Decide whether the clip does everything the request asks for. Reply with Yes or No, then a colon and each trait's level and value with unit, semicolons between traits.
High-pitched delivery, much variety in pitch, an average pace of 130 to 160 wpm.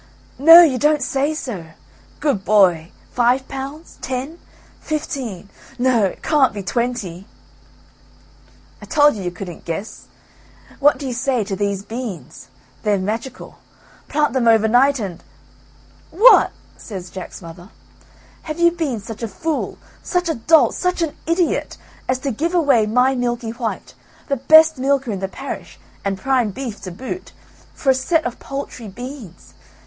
Yes: very high, 250 Hz; wide, 5.9 semitones; average, 155 wpm